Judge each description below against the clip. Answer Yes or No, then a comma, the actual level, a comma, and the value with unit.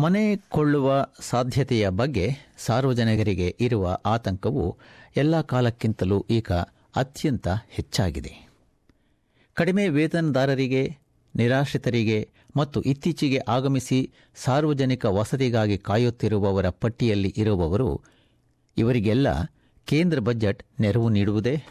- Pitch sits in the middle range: No, low, 120 Hz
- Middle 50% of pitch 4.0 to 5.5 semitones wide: Yes, average, 4.5 semitones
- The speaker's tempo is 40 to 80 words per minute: Yes, average, 75 wpm